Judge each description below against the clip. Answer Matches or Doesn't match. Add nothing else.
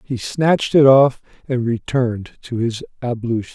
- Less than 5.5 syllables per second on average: Matches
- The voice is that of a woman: Doesn't match